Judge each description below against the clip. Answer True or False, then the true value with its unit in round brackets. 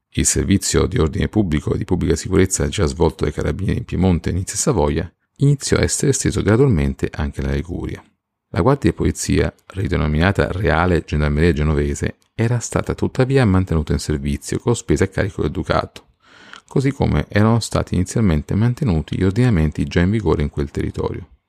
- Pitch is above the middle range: False (90 Hz)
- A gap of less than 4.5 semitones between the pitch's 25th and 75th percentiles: False (5.5 semitones)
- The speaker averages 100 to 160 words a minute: False (170 wpm)